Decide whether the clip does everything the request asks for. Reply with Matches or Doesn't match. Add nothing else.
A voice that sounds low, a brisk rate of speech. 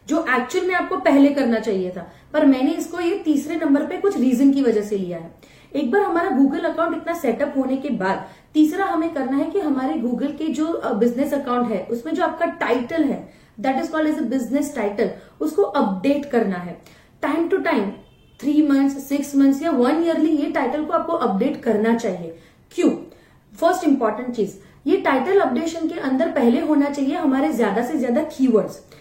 Doesn't match